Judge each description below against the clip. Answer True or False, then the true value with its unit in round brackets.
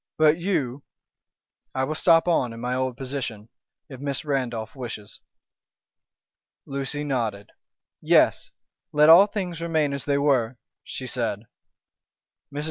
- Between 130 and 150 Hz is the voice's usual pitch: True (135 Hz)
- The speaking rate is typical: False (130 wpm)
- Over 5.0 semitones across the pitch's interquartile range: False (3.7 semitones)